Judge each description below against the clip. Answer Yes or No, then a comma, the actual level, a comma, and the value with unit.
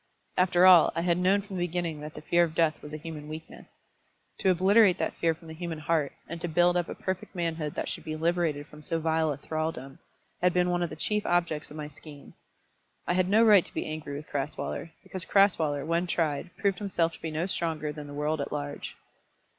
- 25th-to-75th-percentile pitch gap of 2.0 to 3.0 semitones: Yes, narrow, 2.6 semitones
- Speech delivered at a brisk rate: Yes, fast, 230 wpm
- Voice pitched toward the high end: No, medium, 165 Hz